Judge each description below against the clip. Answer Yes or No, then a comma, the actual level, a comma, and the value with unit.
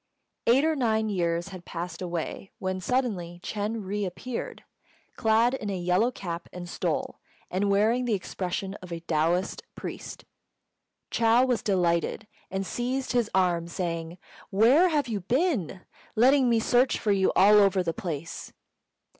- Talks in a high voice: Yes, high, 200 Hz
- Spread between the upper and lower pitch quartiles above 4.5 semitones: Yes, average, 4.9 semitones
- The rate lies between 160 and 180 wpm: No, average, 150 wpm